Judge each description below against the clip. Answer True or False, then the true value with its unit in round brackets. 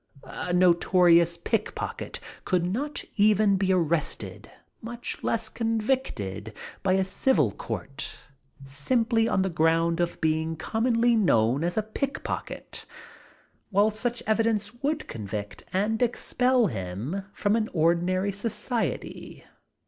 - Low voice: False (190 Hz)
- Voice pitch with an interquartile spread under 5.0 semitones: False (5.4 semitones)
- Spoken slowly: True (115 wpm)